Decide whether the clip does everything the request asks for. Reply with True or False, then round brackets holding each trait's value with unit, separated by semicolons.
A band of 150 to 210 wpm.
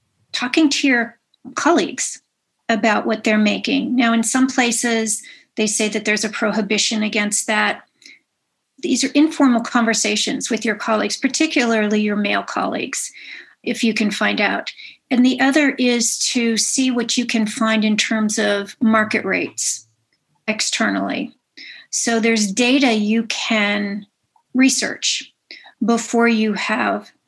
False (135 wpm)